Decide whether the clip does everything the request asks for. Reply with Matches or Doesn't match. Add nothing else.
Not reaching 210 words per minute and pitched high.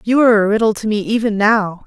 Doesn't match